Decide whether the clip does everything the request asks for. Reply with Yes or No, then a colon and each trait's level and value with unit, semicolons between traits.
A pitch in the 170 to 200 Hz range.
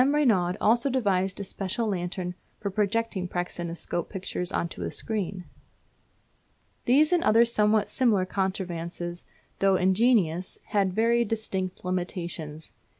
Yes: high, 190 Hz